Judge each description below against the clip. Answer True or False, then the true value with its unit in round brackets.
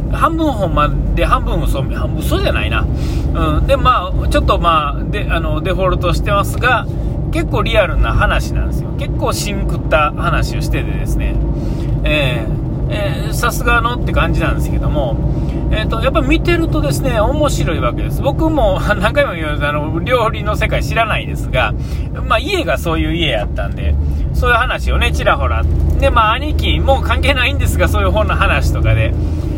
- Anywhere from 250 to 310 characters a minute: False (355 characters per minute)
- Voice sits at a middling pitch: False (80 Hz)